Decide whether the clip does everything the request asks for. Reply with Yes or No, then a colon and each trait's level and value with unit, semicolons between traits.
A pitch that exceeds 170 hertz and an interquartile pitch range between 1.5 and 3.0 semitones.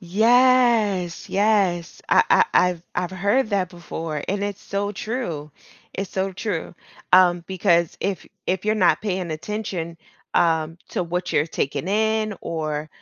No: medium, 185 Hz; average, 3.6 semitones